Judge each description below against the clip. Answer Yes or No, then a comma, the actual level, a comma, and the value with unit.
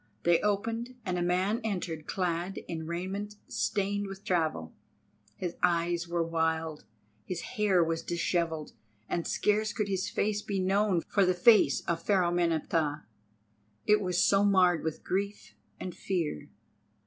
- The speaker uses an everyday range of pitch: Yes, average, 3.2 semitones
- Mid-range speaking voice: Yes, medium, 180 Hz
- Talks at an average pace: Yes, average, 145 wpm